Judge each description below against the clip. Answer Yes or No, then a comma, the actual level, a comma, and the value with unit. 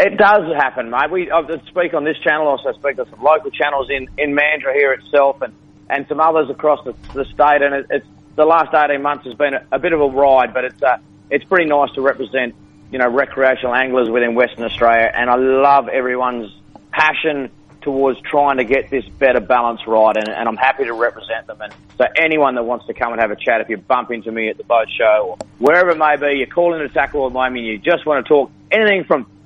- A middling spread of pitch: Yes, average, 3.5 semitones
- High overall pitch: No, medium, 140 Hz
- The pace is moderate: No, fast, 245 wpm